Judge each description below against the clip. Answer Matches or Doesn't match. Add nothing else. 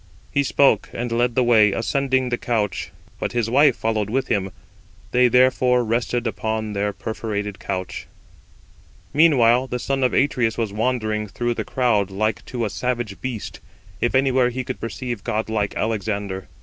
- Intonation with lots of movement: Doesn't match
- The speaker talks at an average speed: Matches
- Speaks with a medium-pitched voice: Doesn't match